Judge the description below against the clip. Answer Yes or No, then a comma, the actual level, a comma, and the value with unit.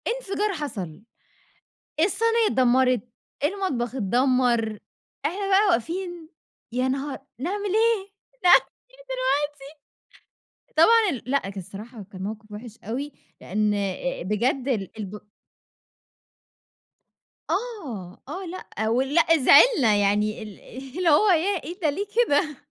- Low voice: No, very high, 275 Hz